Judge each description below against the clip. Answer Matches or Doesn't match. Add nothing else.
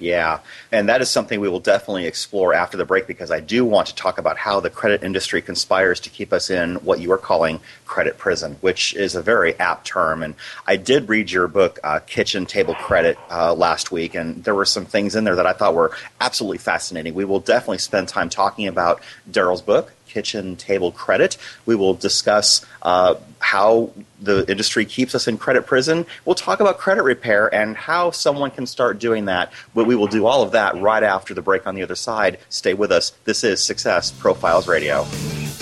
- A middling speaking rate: Doesn't match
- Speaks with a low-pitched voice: Matches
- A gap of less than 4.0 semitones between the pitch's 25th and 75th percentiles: Doesn't match